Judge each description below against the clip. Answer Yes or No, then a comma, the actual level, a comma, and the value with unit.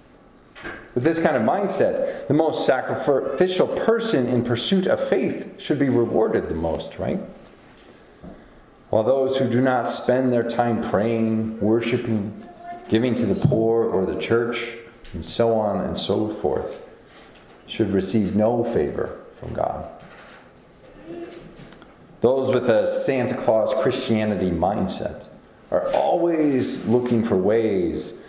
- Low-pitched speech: Yes, low, 125 Hz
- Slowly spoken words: Yes, slow, 125 wpm